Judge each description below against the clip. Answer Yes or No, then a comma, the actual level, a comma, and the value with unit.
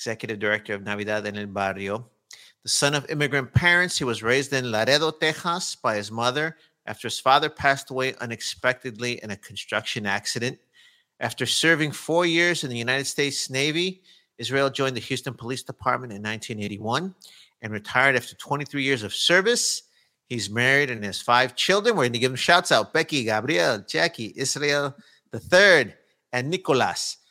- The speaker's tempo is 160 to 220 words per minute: Yes, average, 165 wpm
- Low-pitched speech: Yes, low, 130 Hz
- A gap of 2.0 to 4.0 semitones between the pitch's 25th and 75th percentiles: No, average, 4.7 semitones